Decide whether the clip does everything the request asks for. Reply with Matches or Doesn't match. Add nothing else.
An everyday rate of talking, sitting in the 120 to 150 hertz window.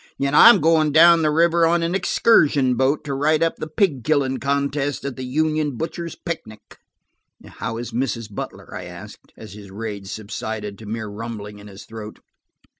Matches